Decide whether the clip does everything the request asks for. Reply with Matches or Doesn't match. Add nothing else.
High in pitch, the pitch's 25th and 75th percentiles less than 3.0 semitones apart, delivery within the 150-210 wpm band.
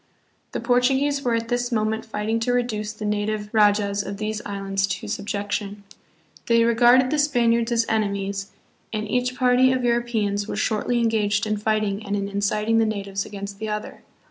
Matches